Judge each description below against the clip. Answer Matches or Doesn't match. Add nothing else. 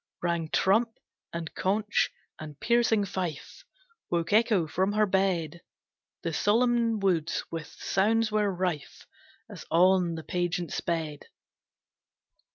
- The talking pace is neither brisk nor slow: Doesn't match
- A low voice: Doesn't match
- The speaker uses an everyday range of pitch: Matches